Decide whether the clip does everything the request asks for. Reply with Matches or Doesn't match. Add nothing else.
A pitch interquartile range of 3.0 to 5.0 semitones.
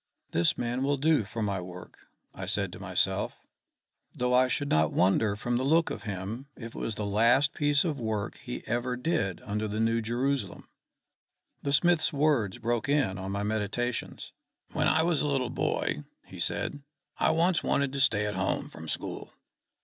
Doesn't match